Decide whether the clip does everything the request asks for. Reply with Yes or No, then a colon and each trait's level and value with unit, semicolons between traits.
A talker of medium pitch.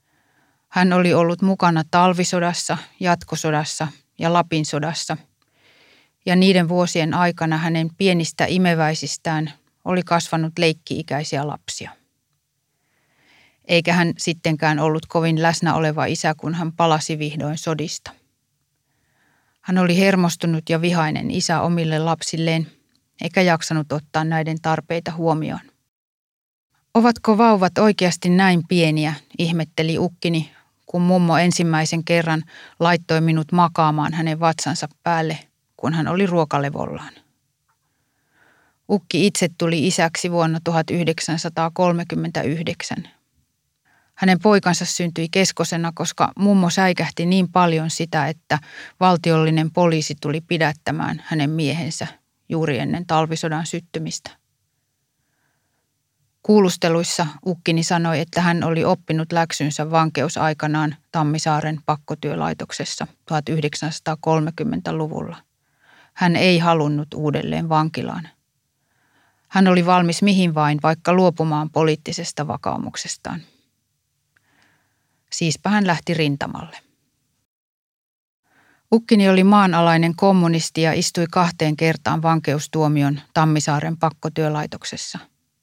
Yes: medium, 165 Hz